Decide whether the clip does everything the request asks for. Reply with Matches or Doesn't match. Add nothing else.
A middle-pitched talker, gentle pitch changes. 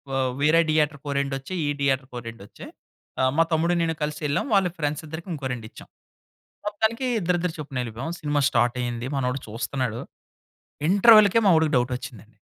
Doesn't match